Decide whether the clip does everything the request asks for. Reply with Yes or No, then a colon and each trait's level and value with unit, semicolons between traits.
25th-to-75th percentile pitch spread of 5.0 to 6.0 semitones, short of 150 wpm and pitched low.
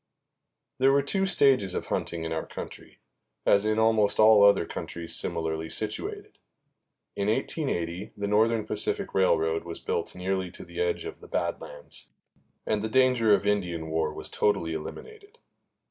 No: wide, 5.5 semitones; average, 160 wpm; low, 105 Hz